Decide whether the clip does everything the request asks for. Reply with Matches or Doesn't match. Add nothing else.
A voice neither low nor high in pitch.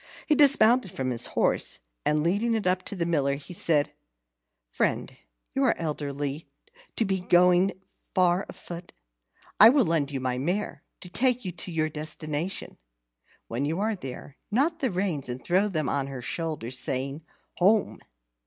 Matches